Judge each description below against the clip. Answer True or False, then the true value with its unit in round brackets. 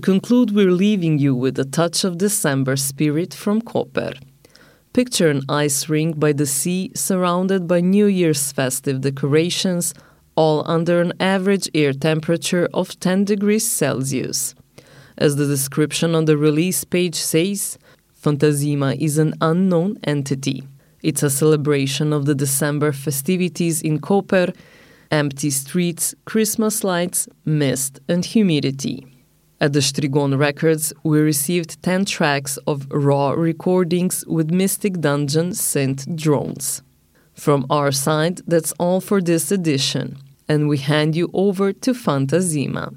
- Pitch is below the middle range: False (155 Hz)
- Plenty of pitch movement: False (3.7 semitones)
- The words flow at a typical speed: False (135 wpm)